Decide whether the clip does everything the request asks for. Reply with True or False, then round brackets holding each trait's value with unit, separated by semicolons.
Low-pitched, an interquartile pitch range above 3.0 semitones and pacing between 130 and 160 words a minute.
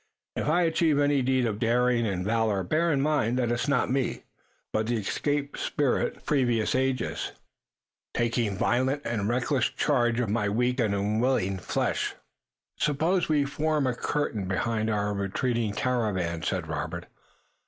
True (120 Hz; 4.4 semitones; 155 wpm)